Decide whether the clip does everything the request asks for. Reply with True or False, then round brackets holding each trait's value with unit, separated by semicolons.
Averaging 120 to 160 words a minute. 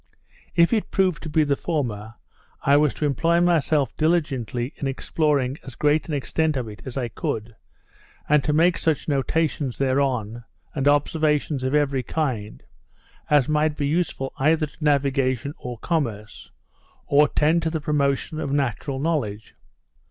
True (155 wpm)